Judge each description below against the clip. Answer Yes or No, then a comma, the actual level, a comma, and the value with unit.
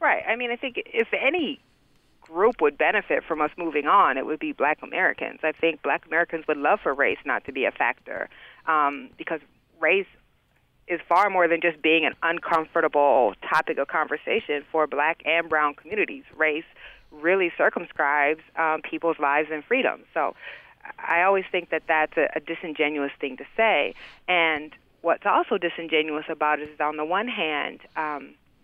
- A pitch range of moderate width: No, narrow, 2.3 semitones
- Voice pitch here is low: No, medium, 160 Hz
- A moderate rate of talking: Yes, average, 175 wpm